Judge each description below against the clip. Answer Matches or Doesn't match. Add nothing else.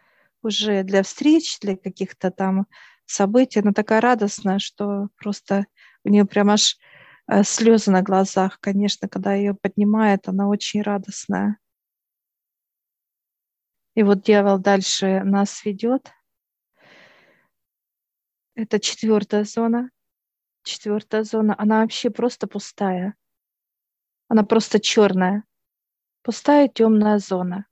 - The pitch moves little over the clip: Matches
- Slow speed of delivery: Matches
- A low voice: Doesn't match